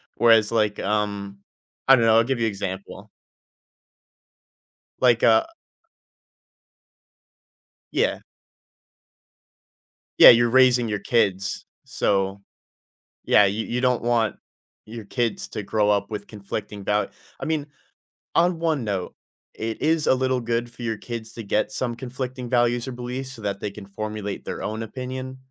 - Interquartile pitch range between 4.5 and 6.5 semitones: No, average, 3.1 semitones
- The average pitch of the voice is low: Yes, low, 115 Hz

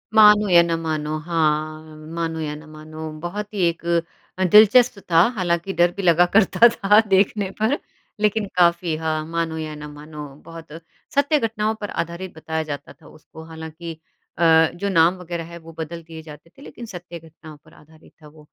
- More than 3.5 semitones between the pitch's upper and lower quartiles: No, average, 3.2 semitones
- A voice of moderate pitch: Yes, medium, 165 Hz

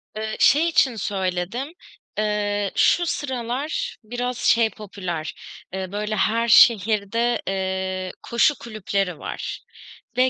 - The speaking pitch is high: Yes, high, 215 Hz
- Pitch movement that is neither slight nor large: Yes, average, 3.9 semitones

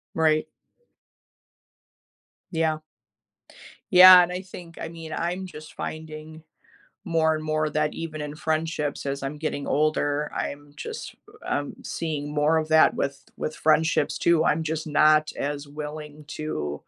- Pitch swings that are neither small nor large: No, narrow, 1.4 semitones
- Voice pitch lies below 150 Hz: No, medium, 155 Hz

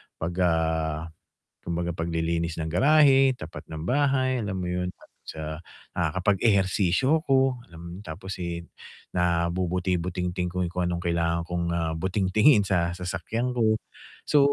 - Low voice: Yes, very low, 90 Hz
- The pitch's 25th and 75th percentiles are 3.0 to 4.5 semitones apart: Yes, average, 3.6 semitones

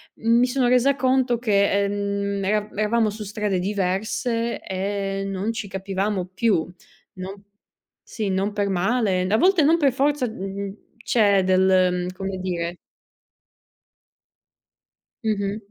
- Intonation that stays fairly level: No, average, 3.0 semitones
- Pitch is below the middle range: No, high, 200 Hz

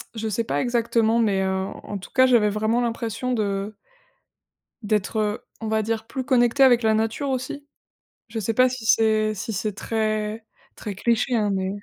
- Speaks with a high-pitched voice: Yes, high, 220 Hz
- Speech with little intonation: Yes, narrow, 2.1 semitones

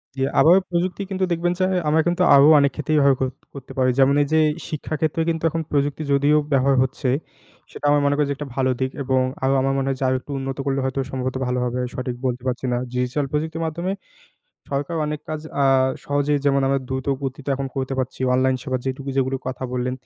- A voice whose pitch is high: No, medium, 140 Hz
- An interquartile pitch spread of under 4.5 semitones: Yes, narrow, 2.4 semitones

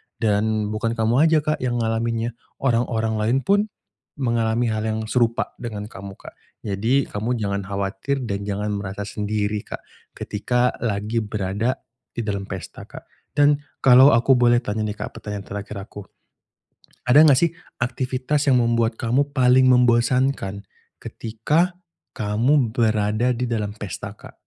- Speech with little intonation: No, average, 3.3 semitones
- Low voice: Yes, low, 115 Hz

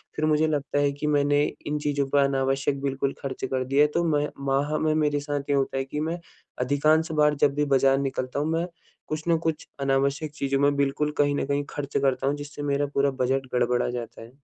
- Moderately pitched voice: Yes, medium, 145 Hz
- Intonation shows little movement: Yes, narrow, 1.5 semitones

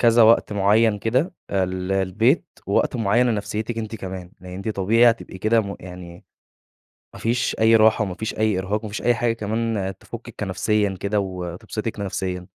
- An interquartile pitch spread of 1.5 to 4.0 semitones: Yes, average, 3.1 semitones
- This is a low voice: Yes, low, 105 Hz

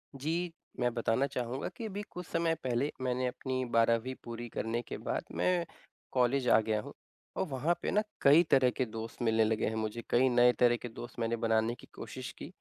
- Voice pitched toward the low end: Yes, low, 125 Hz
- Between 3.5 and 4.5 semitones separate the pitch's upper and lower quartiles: No, average, 3.0 semitones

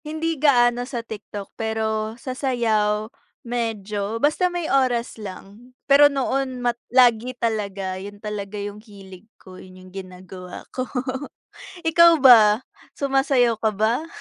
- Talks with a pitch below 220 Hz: No, high, 225 Hz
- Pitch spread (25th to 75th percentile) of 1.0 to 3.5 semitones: No, average, 4.0 semitones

